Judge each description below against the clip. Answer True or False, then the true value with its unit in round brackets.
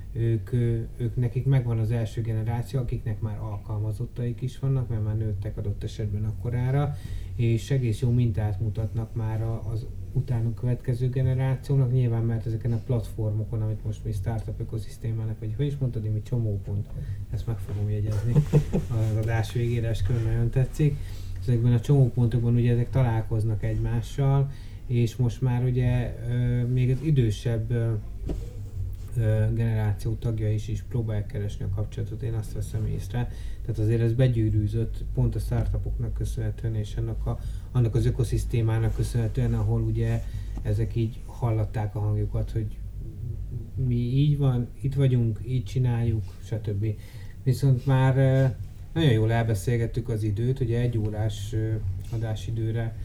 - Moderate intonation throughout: False (2.1 semitones)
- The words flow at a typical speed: True (140 wpm)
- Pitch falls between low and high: False (115 Hz)